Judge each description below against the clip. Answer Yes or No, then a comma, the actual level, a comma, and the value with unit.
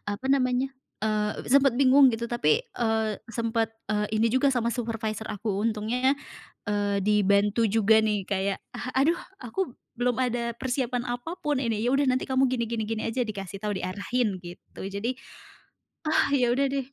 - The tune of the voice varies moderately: Yes, average, 3.4 semitones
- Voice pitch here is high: Yes, high, 230 Hz